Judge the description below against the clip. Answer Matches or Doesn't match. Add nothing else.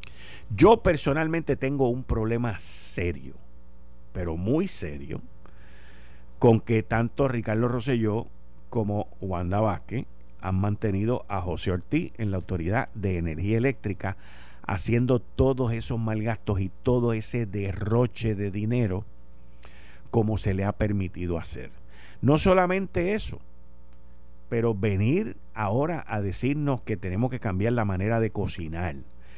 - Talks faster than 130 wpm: Doesn't match